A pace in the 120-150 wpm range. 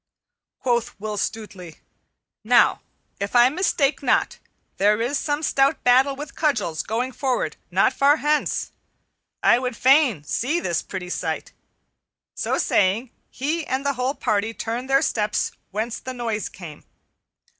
Yes: average, 140 wpm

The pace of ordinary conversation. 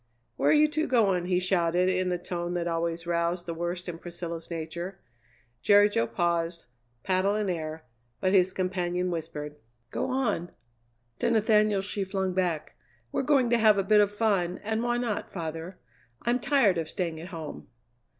Yes: average, 170 wpm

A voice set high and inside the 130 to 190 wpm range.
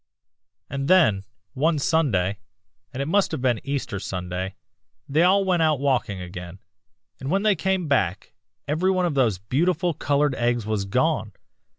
No: medium, 140 Hz; average, 160 wpm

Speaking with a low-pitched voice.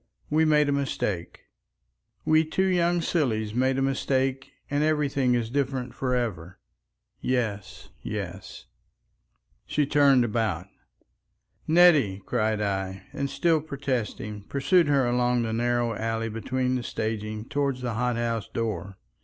Yes: low, 125 Hz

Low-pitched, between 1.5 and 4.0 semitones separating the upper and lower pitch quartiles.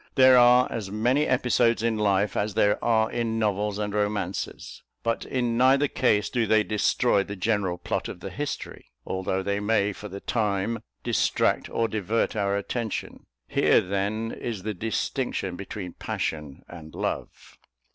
Yes: low, 105 Hz; average, 2.7 semitones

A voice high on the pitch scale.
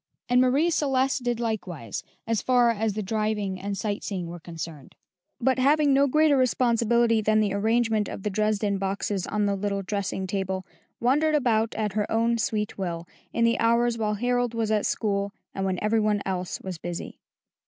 Yes: high, 215 Hz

